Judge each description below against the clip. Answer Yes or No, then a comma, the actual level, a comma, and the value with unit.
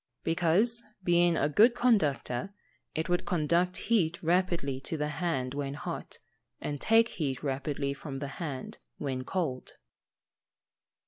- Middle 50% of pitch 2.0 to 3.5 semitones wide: No, average, 4.4 semitones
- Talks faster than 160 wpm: No, slow, 135 wpm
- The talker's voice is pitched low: No, medium, 160 Hz